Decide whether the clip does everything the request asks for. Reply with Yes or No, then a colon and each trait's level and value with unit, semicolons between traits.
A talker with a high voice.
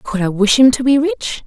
Yes: high, 245 Hz